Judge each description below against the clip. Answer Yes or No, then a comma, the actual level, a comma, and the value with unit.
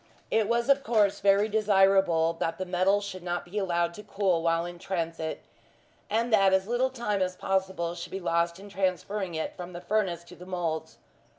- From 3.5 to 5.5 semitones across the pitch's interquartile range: No, average, 2.9 semitones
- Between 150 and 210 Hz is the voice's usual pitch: Yes, high, 190 Hz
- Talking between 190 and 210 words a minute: Yes, average, 195 wpm